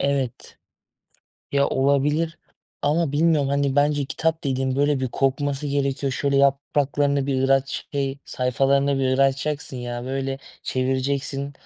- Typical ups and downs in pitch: No, narrow, 1.2 semitones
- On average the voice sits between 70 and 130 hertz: No, medium, 140 Hz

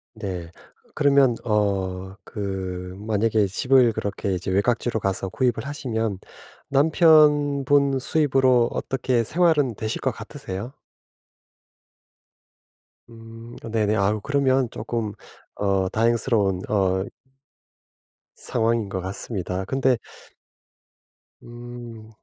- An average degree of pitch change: Yes, average, 4.9 semitones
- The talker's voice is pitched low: Yes, low, 115 Hz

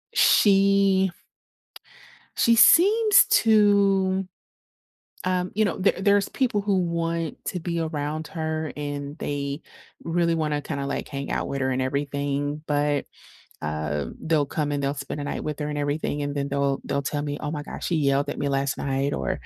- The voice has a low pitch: No, medium, 150 Hz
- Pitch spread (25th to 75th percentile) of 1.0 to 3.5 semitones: No, average, 4.5 semitones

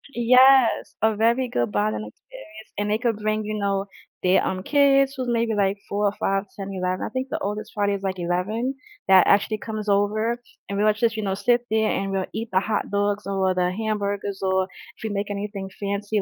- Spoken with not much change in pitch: Yes, narrow, 2.3 semitones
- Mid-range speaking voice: No, high, 205 Hz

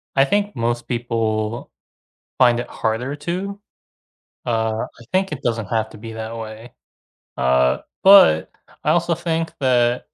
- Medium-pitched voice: No, low, 120 Hz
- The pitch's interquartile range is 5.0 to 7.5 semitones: Yes, average, 5.3 semitones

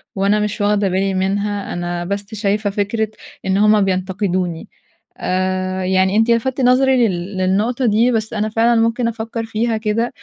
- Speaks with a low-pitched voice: No, high, 205 Hz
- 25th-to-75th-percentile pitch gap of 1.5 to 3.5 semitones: Yes, average, 3.1 semitones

